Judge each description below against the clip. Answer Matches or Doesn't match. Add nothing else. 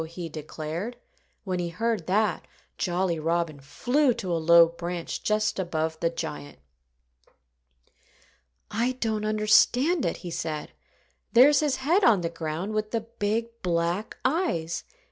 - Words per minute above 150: Doesn't match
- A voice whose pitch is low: Doesn't match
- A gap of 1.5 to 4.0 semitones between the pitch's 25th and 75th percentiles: Doesn't match